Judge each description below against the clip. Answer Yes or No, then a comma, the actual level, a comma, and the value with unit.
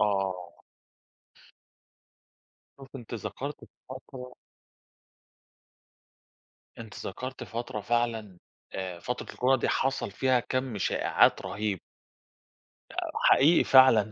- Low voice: Yes, low, 120 Hz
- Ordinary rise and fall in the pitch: Yes, average, 4.2 semitones